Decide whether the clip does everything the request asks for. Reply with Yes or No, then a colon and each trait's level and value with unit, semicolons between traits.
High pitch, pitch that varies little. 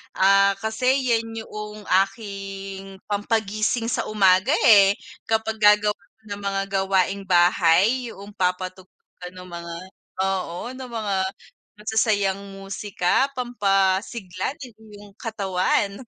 Yes: high, 200 Hz; narrow, 2.2 semitones